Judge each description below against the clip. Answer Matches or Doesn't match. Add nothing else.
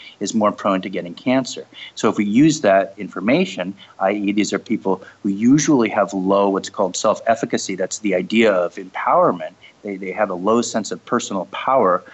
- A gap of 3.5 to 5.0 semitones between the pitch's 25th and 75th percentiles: Doesn't match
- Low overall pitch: Matches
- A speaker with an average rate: Matches